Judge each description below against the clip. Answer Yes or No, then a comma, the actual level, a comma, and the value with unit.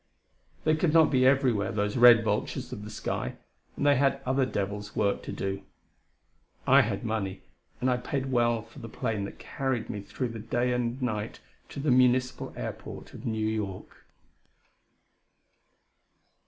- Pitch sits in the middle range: No, low, 120 Hz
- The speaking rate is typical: Yes, average, 165 wpm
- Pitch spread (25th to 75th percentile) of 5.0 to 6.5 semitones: No, average, 3.6 semitones